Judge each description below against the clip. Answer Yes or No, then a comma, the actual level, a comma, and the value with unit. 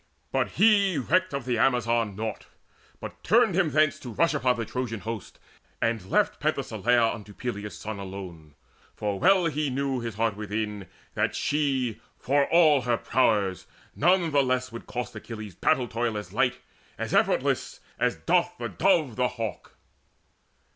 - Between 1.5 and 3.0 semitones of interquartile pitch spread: No, average, 4.6 semitones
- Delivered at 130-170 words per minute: Yes, average, 160 wpm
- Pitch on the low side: Yes, low, 120 Hz